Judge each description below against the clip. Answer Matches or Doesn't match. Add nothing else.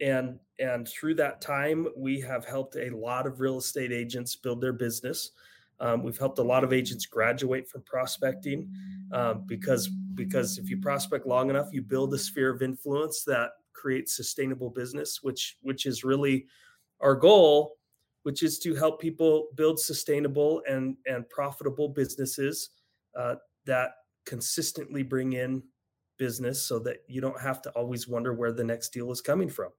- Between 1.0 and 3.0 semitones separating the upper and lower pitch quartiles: Matches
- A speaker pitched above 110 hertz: Matches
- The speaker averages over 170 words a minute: Doesn't match